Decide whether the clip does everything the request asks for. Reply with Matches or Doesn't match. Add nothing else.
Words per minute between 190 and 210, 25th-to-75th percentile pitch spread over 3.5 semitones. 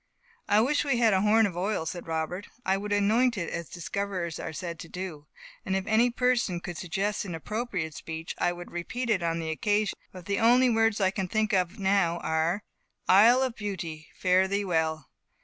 Matches